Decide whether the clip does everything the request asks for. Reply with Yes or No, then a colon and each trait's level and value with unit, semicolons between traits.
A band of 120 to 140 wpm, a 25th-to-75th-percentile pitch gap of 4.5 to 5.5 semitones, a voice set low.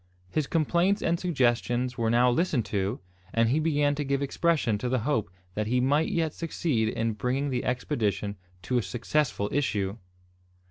No: average, 170 wpm; average, 4.8 semitones; low, 125 Hz